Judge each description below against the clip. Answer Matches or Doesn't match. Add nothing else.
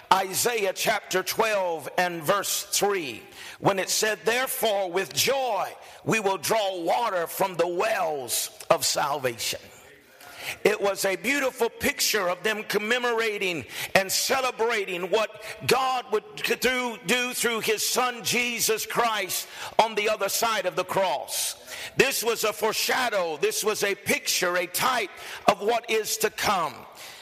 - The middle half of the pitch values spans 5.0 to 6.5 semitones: Doesn't match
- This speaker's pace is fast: Doesn't match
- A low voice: Doesn't match